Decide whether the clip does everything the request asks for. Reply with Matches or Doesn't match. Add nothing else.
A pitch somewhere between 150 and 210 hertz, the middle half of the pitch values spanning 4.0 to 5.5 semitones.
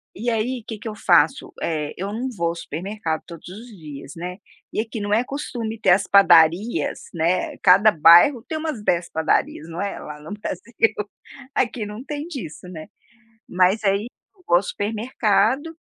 Matches